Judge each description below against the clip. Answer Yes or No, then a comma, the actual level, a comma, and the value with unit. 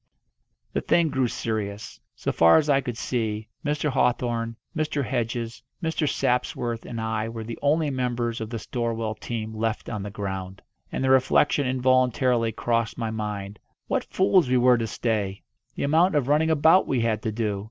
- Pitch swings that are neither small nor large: Yes, average, 3.2 semitones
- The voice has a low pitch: Yes, low, 120 Hz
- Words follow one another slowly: No, average, 175 wpm